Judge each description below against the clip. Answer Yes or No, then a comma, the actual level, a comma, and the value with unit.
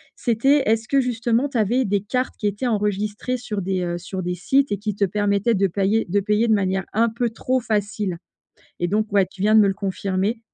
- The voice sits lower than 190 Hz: No, high, 210 Hz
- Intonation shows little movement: No, average, 3.0 semitones